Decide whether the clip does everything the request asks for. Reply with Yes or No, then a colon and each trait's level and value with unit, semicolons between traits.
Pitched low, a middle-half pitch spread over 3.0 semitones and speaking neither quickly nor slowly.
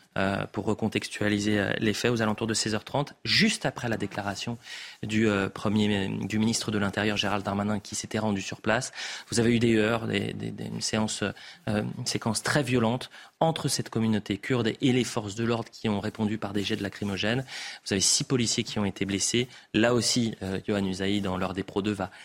No: low, 110 Hz; narrow, 2.4 semitones; average, 200 wpm